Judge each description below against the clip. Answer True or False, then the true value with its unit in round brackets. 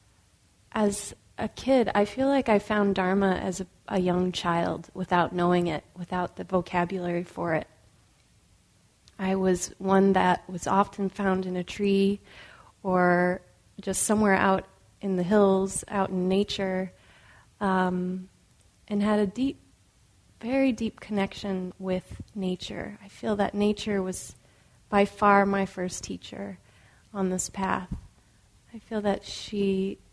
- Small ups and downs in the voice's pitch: True (2.0 semitones)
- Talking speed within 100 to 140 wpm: True (135 wpm)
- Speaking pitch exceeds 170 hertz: True (190 Hz)